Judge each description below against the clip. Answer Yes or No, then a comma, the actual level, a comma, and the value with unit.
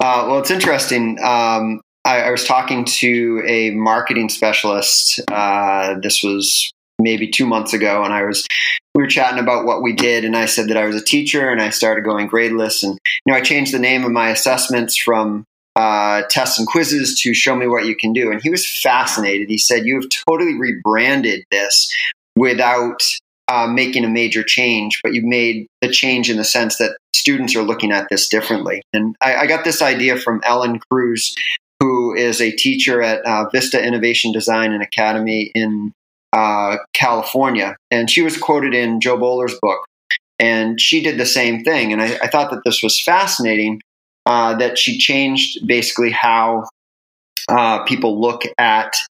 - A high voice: No, low, 115 Hz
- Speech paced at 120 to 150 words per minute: No, average, 185 wpm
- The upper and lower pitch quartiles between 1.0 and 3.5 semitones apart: Yes, narrow, 2.4 semitones